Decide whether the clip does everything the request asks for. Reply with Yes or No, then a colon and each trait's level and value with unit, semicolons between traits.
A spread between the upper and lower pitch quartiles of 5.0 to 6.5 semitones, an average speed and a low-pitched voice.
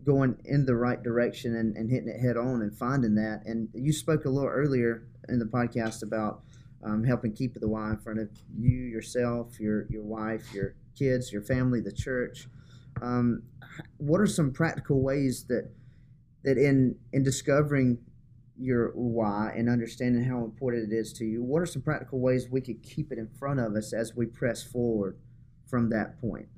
No: narrow, 2.6 semitones; average, 190 wpm; low, 120 Hz